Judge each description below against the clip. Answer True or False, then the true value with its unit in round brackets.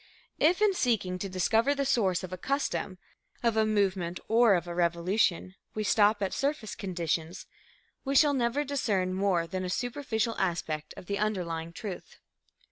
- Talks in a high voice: True (200 Hz)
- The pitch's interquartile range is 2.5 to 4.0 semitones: False (4.6 semitones)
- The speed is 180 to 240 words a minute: False (165 wpm)